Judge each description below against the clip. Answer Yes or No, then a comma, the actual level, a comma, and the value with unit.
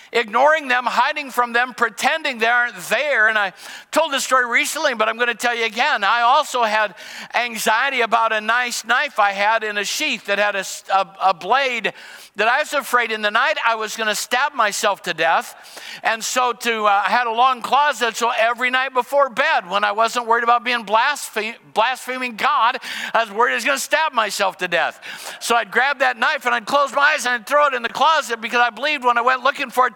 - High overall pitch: Yes, high, 240 Hz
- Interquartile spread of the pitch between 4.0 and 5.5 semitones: No, average, 3.1 semitones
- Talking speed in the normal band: No, fast, 230 wpm